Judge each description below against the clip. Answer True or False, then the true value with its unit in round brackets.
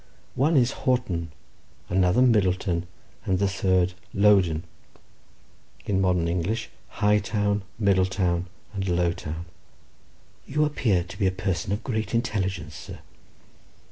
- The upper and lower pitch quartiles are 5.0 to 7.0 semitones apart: False (3.0 semitones)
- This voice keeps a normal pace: False (110 wpm)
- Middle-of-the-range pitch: False (95 Hz)